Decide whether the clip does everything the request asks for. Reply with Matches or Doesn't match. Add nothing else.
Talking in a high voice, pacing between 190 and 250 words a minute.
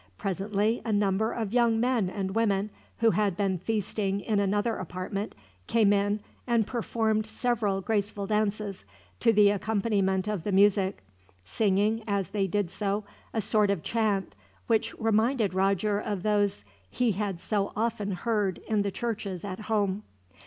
Doesn't match